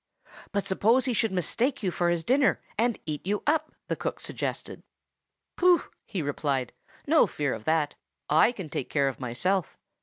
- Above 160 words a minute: Yes, average, 175 wpm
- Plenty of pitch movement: Yes, wide, 8.3 semitones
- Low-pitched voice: No, medium, 185 Hz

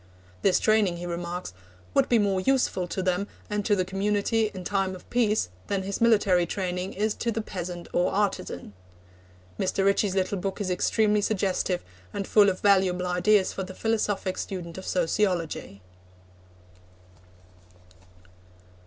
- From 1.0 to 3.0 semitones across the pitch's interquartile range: Yes, narrow, 2.4 semitones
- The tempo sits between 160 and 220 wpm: No, average, 145 wpm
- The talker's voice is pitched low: No, high, 190 Hz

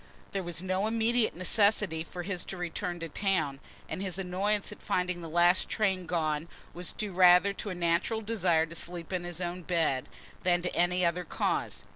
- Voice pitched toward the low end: No, medium, 180 Hz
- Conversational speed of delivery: Yes, average, 185 wpm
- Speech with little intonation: Yes, narrow, 2.1 semitones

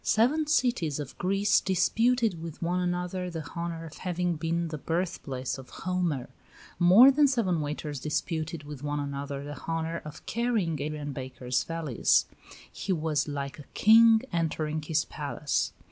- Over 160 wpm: No, average, 150 wpm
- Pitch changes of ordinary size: Yes, average, 3.7 semitones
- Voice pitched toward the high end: No, medium, 165 Hz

